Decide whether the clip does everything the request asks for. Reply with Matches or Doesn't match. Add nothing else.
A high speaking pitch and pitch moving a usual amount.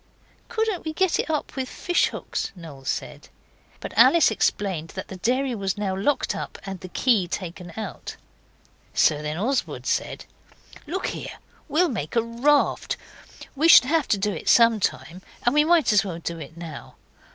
Doesn't match